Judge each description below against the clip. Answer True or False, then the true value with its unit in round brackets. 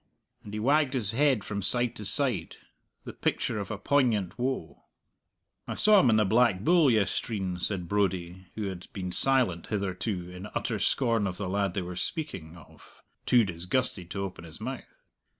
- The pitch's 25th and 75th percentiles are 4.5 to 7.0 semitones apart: True (5.0 semitones)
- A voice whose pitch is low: True (100 Hz)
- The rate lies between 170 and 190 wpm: True (180 wpm)